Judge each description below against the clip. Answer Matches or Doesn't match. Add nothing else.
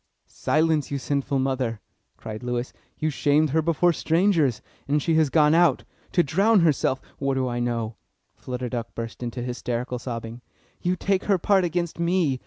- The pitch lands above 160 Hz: Doesn't match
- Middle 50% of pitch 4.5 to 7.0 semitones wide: Matches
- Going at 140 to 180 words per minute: Matches